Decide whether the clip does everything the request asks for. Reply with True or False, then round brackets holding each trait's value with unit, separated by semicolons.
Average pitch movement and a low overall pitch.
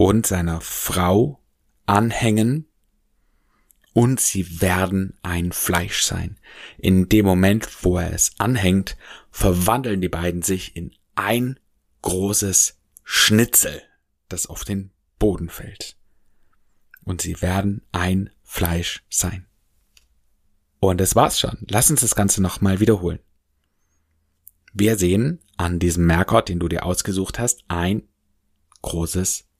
True (3.3 semitones; 95 Hz)